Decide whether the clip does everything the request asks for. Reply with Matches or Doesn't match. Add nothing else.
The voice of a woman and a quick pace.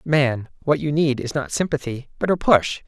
Doesn't match